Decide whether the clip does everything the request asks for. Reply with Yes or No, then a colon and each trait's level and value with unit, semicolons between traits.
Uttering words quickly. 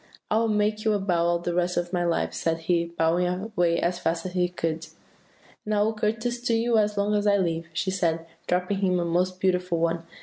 Yes: fast, 235 wpm